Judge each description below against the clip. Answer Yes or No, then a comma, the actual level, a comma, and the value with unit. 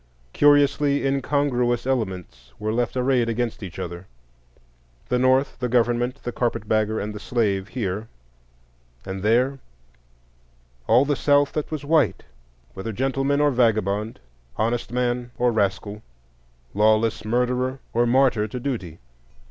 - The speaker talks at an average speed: No, slow, 125 wpm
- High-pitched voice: No, low, 120 Hz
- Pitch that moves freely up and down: No, average, 3.8 semitones